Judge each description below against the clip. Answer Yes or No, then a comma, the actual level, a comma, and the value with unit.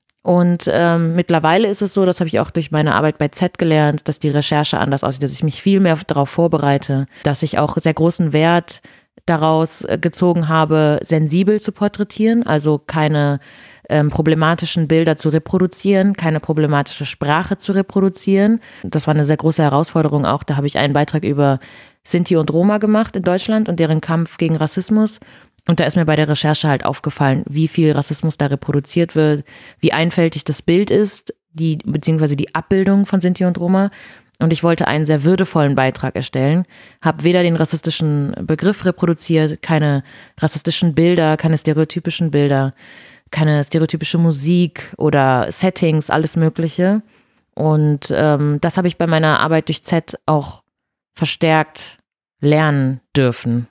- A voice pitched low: No, medium, 160 Hz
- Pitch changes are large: No, narrow, 2.6 semitones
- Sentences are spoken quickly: No, average, 160 wpm